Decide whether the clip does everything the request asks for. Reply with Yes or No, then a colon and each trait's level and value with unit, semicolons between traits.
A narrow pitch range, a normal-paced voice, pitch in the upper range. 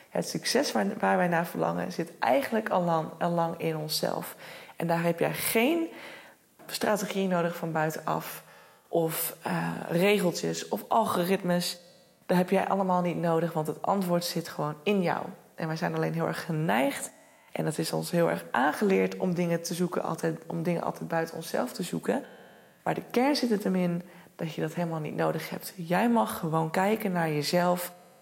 No: narrow, 2.3 semitones; average, 175 wpm; medium, 175 Hz